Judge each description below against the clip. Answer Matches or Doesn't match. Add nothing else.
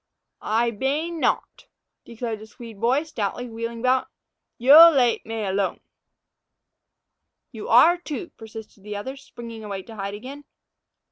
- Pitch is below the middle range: Doesn't match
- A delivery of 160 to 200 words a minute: Doesn't match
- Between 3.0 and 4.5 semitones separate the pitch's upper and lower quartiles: Matches